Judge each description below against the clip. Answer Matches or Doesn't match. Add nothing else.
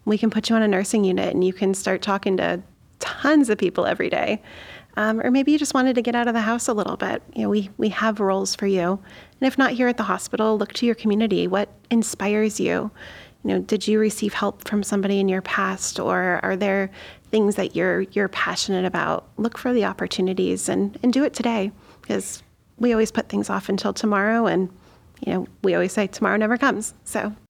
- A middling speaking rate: Doesn't match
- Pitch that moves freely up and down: Doesn't match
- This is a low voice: Doesn't match